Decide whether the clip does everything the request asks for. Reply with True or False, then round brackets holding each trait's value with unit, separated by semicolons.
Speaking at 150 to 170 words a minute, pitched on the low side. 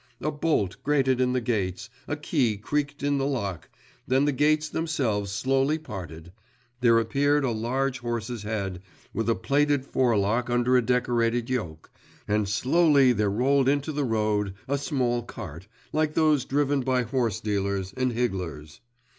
True (155 wpm; 125 Hz)